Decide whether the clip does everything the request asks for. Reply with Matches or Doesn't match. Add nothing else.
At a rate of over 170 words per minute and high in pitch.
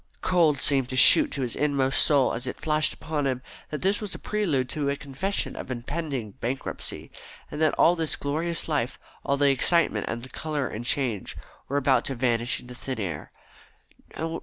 Doesn't match